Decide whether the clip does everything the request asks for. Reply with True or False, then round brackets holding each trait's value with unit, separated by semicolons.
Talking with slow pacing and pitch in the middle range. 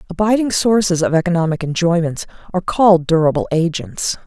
True (125 wpm; 175 Hz)